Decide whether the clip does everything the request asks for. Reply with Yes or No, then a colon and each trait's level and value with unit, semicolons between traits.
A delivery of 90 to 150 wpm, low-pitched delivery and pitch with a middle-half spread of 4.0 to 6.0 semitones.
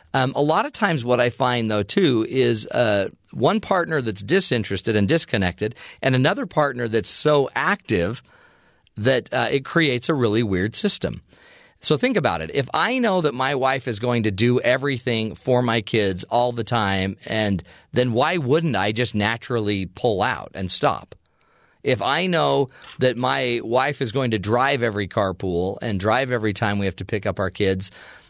No: average, 185 wpm; low, 120 Hz; average, 4.5 semitones